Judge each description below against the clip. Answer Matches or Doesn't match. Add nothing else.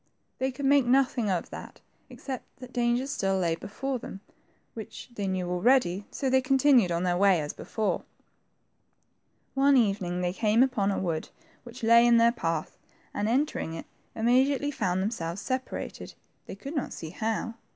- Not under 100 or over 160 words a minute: Doesn't match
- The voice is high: Matches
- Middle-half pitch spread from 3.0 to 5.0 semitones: Doesn't match